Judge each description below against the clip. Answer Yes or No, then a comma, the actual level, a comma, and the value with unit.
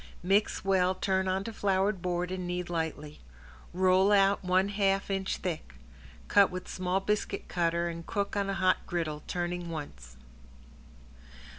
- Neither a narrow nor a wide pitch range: No, narrow, 2.1 semitones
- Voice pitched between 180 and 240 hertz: Yes, medium, 185 Hz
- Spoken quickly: No, average, 145 wpm